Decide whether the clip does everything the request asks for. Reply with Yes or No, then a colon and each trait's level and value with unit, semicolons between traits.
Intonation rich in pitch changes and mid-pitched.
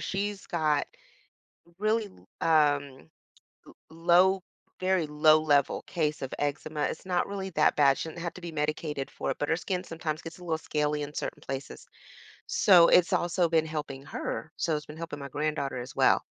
No: average, 2.9 semitones; medium, 155 Hz